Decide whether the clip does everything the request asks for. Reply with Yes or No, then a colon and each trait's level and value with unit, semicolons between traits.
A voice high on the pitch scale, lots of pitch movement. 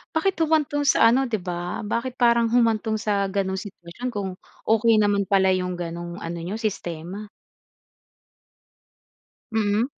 No: high, 210 Hz; average, 4.1 semitones